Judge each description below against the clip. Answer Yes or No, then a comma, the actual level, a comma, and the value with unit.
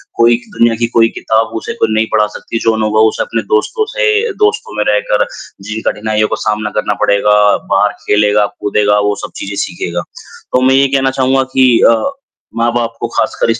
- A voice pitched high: No, low, 115 Hz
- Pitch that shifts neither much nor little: Yes, average, 3.9 semitones